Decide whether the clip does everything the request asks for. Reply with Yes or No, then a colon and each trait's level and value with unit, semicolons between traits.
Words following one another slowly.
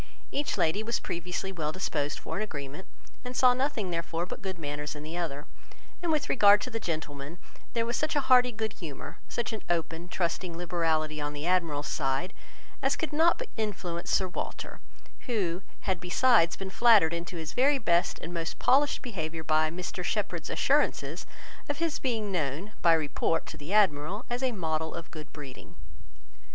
No: average, 180 wpm